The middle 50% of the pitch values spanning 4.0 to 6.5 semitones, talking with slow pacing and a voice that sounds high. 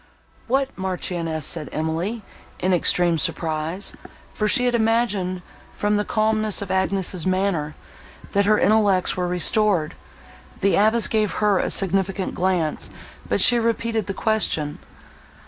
No: average, 3.4 semitones; slow, 130 wpm; high, 195 Hz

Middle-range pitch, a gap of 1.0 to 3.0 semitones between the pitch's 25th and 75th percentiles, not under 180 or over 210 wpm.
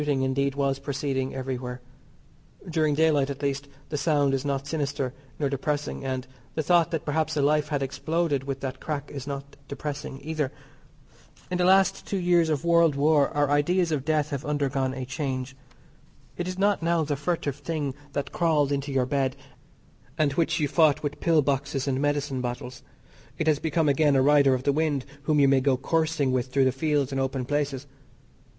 Yes: medium, 145 Hz; narrow, 2.4 semitones; average, 190 wpm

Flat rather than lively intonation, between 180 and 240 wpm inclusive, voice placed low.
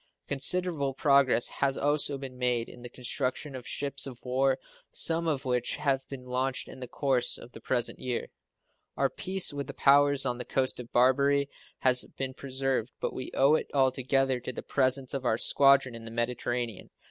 Yes: narrow, 1.9 semitones; average, 185 wpm; low, 130 Hz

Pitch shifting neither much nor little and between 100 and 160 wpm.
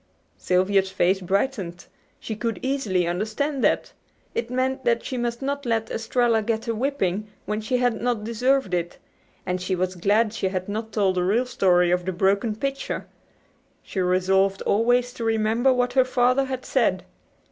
No: average, 4.6 semitones; average, 170 wpm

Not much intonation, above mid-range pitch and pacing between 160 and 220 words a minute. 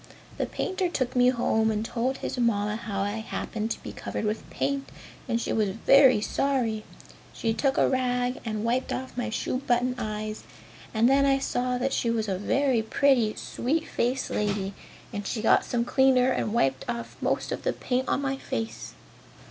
No: average, 3.3 semitones; high, 235 Hz; average, 190 wpm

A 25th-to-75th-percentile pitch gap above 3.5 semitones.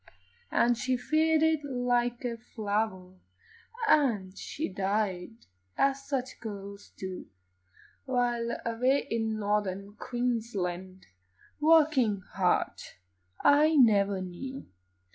Yes: average, 4.7 semitones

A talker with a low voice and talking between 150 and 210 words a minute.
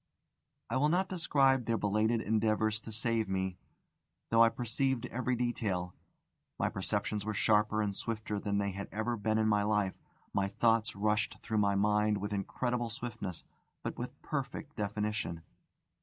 Yes: low, 110 Hz; average, 155 wpm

